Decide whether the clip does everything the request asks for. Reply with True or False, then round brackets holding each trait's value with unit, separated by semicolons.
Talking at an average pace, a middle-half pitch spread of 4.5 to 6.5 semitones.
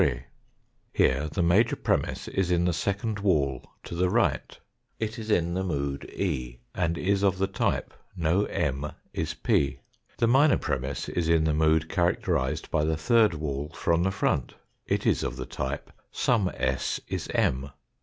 True (170 wpm; 5.0 semitones)